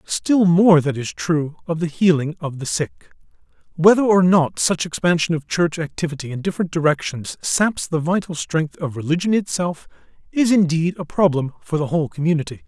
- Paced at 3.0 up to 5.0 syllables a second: No, 5.2 syllables/s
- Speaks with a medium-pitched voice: Yes, medium, 165 Hz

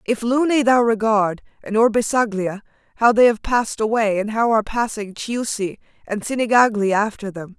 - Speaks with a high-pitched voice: Yes, high, 220 Hz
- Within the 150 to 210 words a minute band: Yes, average, 160 wpm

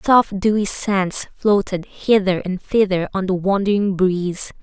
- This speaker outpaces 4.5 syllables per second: No, 4.2 syllables/s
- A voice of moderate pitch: No, high, 195 Hz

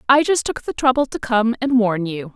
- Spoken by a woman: Yes, female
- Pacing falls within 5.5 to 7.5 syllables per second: No, 5.2 syllables/s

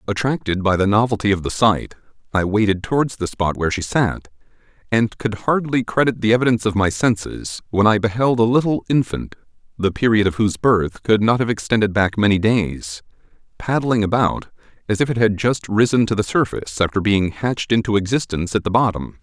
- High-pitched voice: No, low, 105 Hz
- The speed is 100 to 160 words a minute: No, average, 190 wpm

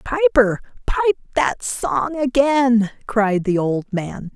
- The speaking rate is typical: No, slow, 125 wpm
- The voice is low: No, high, 240 Hz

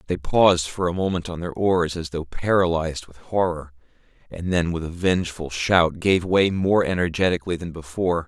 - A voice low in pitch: Yes, very low, 85 Hz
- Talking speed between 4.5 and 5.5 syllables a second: Yes, 5.3 syllables/s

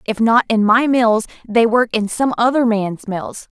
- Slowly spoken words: No, average, 200 wpm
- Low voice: No, high, 230 Hz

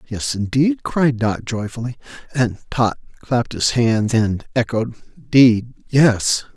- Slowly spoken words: Yes, slow, 130 wpm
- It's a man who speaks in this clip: Yes, male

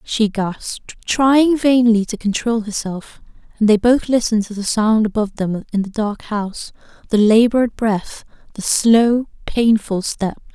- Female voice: Yes, female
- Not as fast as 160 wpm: Yes, average, 150 wpm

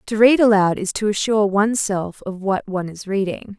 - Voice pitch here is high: Yes, high, 200 Hz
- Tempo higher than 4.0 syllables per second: Yes, 5.5 syllables/s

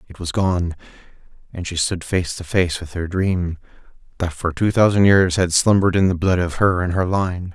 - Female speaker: No, male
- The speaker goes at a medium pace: No, fast, 215 wpm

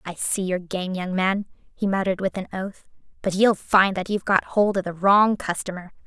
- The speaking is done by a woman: Yes, female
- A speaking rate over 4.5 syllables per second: Yes, 5.2 syllables/s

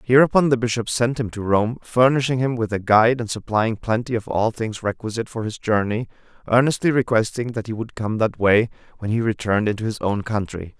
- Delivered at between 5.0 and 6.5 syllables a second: Yes, 5.7 syllables/s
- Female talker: No, male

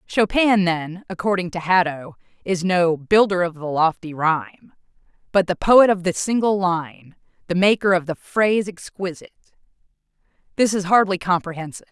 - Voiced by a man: No, female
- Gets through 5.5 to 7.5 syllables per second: No, 5.0 syllables/s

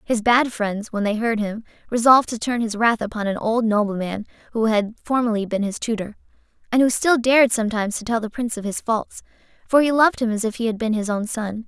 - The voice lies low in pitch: No, high, 225 Hz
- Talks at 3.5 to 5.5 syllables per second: No, 6.0 syllables/s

